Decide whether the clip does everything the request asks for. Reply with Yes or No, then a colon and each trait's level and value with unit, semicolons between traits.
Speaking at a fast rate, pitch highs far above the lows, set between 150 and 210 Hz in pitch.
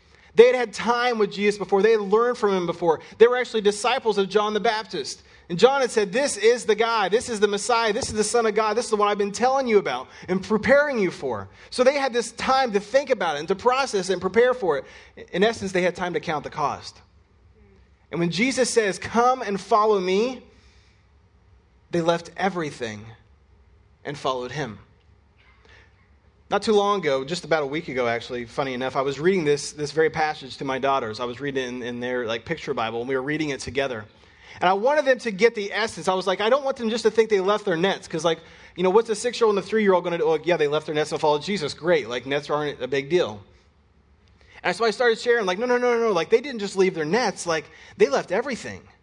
Yes: fast, 245 wpm; wide, 8.6 semitones; high, 190 Hz